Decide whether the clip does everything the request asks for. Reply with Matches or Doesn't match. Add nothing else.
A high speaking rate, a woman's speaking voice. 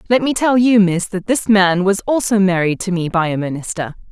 Matches